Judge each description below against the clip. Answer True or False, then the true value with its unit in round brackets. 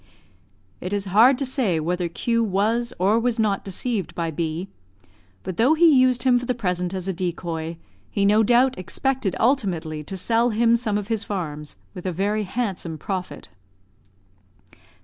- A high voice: True (200 Hz)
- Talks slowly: False (170 wpm)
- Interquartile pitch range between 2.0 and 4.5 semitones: False (4.9 semitones)